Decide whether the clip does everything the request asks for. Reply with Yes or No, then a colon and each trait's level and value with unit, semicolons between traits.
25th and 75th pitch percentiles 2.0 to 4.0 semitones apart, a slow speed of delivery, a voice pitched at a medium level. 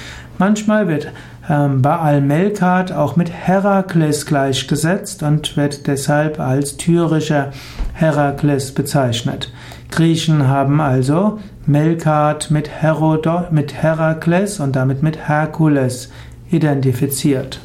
Yes: narrow, 2.6 semitones; slow, 95 wpm; medium, 150 Hz